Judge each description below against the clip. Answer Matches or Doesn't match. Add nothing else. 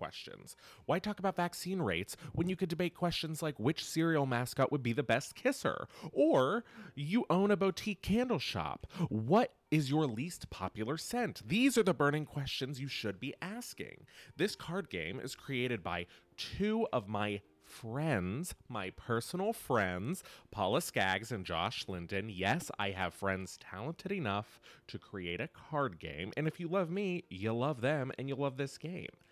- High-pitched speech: Doesn't match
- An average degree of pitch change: Doesn't match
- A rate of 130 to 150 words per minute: Doesn't match